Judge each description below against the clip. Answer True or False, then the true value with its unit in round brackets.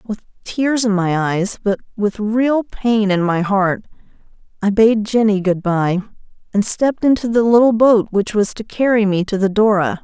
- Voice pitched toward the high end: True (210 Hz)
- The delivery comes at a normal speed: True (185 wpm)